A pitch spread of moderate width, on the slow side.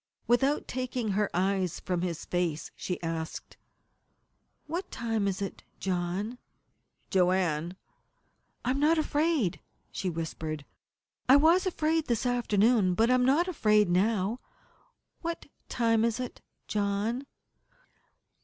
No: wide, 5.8 semitones; slow, 125 wpm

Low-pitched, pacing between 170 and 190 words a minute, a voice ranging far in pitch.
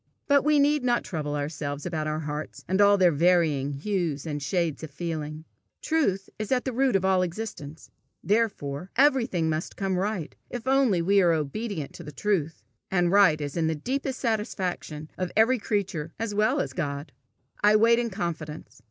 No: medium, 180 Hz; average, 180 wpm; wide, 6.0 semitones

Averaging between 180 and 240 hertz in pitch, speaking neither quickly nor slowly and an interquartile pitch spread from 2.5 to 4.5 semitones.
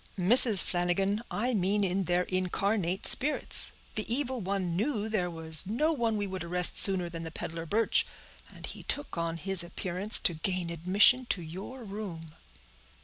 Yes: high, 190 Hz; average, 165 wpm; average, 3.8 semitones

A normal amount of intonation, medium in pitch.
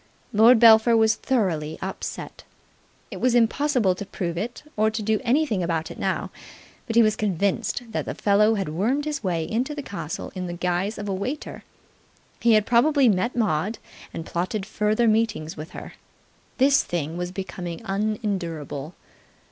No: average, 4.6 semitones; high, 210 Hz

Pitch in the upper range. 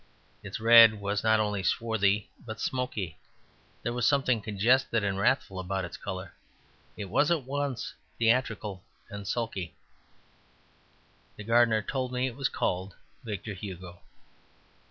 No: low, 110 Hz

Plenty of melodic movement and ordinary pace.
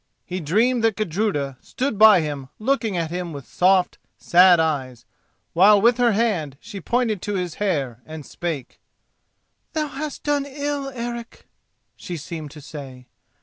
Yes: wide, 7.3 semitones; average, 150 wpm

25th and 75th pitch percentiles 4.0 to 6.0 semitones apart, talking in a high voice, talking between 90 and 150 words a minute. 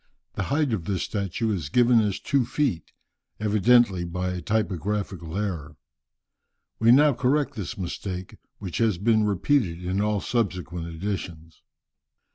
No: average, 4.5 semitones; low, 100 Hz; slow, 135 wpm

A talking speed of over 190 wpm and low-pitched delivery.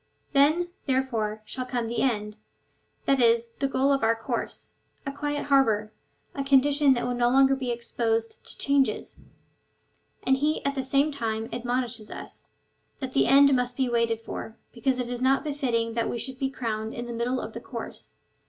No: average, 200 wpm; very high, 250 Hz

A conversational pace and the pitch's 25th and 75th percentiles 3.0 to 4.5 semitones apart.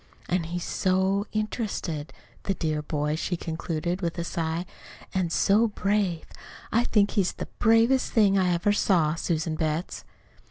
Yes: average, 150 wpm; average, 3.8 semitones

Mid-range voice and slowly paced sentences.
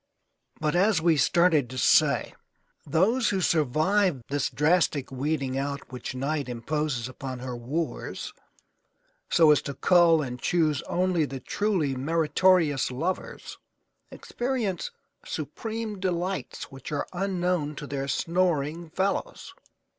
Yes: medium, 155 Hz; slow, 120 wpm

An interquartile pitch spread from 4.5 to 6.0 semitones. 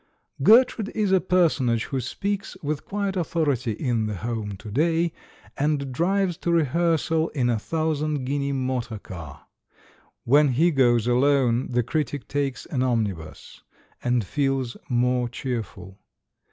Yes: average, 5.1 semitones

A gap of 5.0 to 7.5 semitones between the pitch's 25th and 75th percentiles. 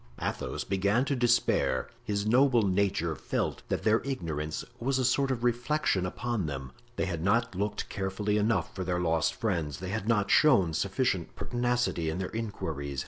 Yes: wide, 5.5 semitones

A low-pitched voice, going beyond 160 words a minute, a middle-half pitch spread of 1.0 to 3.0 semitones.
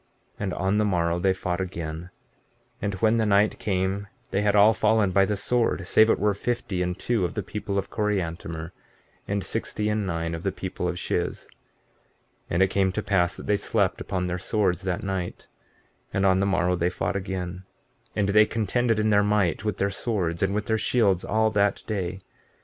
Yes: low, 100 Hz; fast, 205 wpm; narrow, 2.6 semitones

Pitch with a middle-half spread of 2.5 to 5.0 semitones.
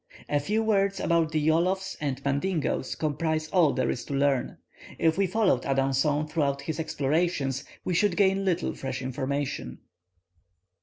Yes: average, 4.6 semitones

